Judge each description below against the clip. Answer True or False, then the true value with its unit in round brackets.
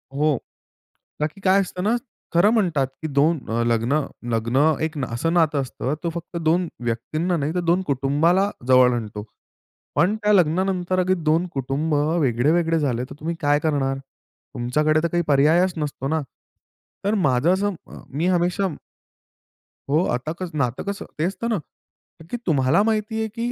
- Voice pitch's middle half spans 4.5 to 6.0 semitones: True (5.0 semitones)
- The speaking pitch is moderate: True (155 Hz)